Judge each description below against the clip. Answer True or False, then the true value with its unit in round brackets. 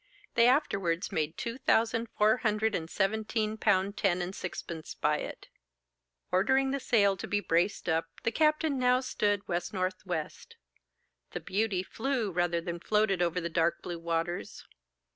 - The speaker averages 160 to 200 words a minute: False (150 wpm)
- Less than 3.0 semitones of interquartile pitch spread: False (4.6 semitones)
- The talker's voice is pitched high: True (195 Hz)